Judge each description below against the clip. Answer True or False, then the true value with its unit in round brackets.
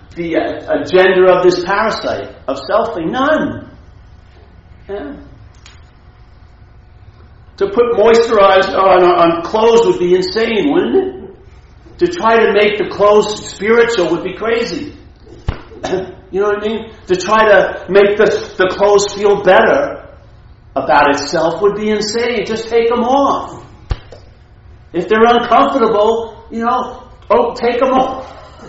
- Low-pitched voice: False (205 Hz)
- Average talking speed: False (130 wpm)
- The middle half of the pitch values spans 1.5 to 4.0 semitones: False (5.1 semitones)